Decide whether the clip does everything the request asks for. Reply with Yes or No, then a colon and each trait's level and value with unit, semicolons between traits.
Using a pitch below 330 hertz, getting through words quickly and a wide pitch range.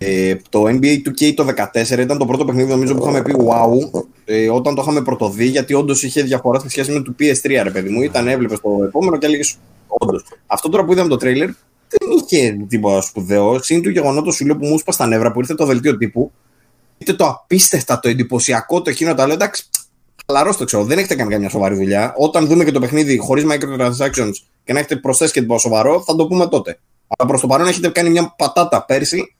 No: low, 135 Hz; fast, 215 wpm; average, 4.3 semitones